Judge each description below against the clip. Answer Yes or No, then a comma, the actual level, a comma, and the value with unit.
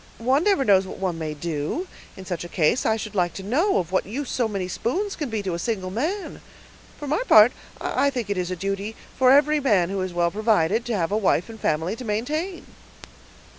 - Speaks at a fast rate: Yes, fast, 230 wpm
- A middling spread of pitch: No, wide, 6.0 semitones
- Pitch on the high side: Yes, high, 210 Hz